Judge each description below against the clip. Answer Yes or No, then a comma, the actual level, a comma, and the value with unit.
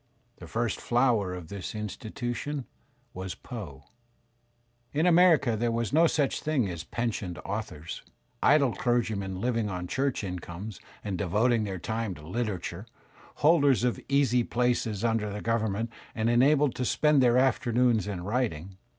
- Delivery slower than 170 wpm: Yes, average, 145 wpm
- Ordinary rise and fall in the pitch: Yes, average, 4.2 semitones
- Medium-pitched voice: No, low, 115 Hz